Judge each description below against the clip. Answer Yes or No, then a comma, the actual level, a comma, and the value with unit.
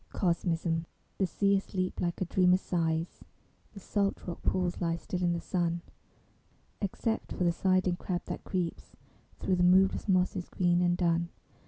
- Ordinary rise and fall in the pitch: No, narrow, 1.5 semitones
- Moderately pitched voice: Yes, medium, 180 Hz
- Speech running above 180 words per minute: No, average, 160 wpm